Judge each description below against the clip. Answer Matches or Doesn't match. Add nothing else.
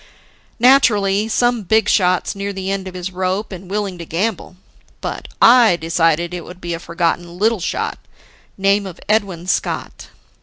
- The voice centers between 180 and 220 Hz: Matches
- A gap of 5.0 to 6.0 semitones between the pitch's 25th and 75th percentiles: Doesn't match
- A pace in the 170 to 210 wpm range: Doesn't match